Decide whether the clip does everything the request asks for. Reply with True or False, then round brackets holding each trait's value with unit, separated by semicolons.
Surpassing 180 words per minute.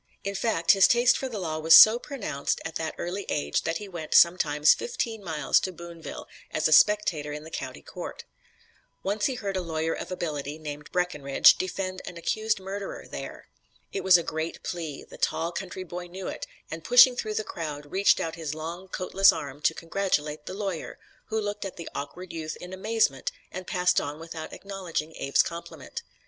True (190 wpm)